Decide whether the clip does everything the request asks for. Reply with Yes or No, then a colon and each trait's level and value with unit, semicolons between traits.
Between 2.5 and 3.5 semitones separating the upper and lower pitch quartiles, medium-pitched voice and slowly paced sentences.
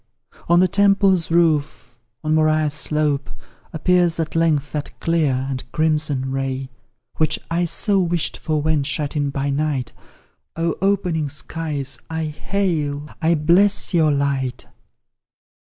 Yes: average, 2.8 semitones; medium, 155 Hz; slow, 130 wpm